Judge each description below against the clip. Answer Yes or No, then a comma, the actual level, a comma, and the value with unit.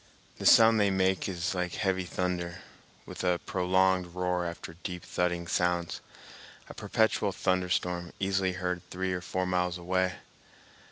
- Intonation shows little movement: Yes, narrow, 1.0 semitones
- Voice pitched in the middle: No, very low, 90 Hz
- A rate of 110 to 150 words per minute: Yes, slow, 135 wpm